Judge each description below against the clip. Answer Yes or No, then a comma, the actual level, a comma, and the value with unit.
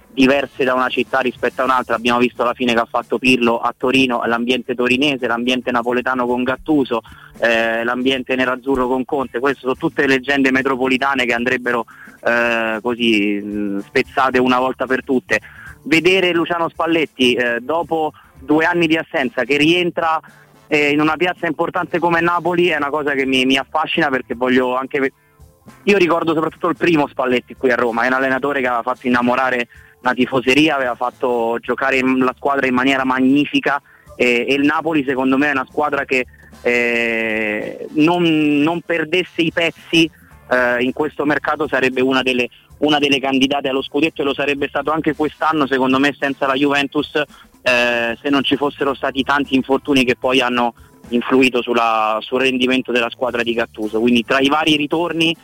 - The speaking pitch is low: Yes, low, 130 Hz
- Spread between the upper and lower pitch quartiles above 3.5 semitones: No, average, 3.2 semitones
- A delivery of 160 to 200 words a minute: Yes, fast, 170 wpm